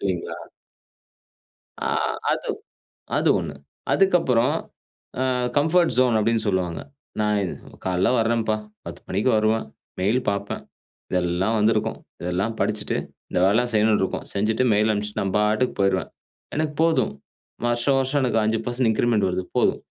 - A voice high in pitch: No, low, 110 Hz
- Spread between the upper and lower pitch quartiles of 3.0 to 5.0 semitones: Yes, average, 3.5 semitones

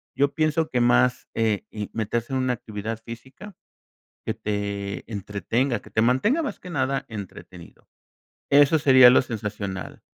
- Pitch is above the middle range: No, low, 120 Hz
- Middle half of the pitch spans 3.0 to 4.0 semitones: No, average, 4.5 semitones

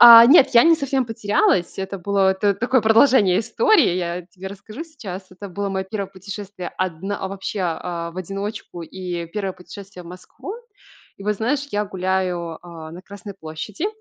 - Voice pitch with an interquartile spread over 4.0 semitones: No, average, 3.1 semitones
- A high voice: Yes, high, 195 Hz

